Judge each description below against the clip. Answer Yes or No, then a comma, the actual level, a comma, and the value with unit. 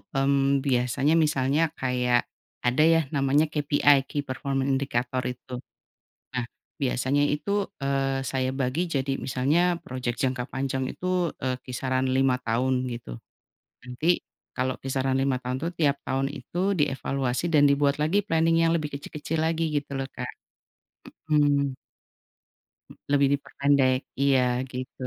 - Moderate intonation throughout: No, narrow, 1.8 semitones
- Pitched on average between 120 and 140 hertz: Yes, low, 135 Hz